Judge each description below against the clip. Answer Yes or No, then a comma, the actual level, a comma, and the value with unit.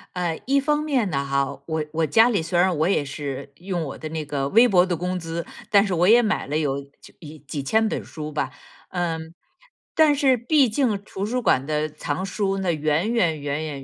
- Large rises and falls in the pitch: Yes, wide, 5.9 semitones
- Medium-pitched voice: Yes, medium, 170 Hz